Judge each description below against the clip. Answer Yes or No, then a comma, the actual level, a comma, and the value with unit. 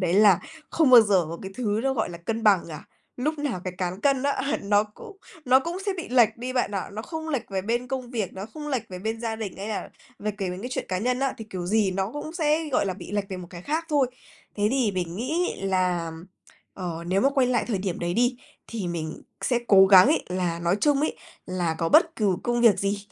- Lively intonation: Yes, wide, 5.8 semitones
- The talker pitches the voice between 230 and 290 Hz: No, high, 215 Hz